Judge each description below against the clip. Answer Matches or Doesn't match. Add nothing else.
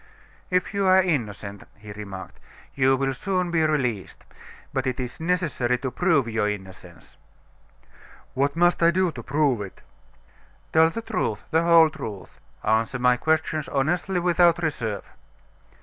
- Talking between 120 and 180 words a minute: Matches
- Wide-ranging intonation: Matches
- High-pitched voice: Doesn't match